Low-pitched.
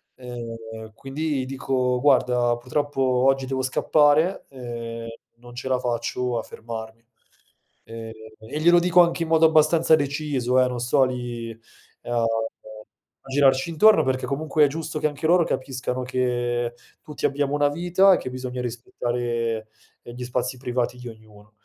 Yes: low, 130 Hz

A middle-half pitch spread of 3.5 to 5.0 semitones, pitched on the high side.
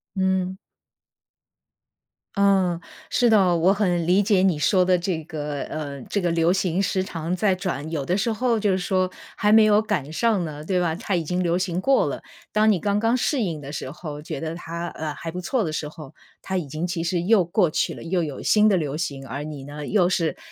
No: average, 3.8 semitones; medium, 180 Hz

